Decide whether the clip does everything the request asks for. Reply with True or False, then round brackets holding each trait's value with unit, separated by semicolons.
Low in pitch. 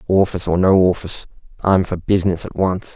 True (90 Hz)